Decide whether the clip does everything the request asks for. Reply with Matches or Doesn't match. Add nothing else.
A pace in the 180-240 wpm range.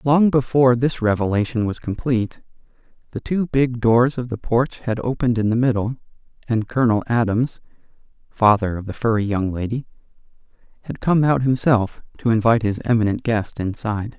Doesn't match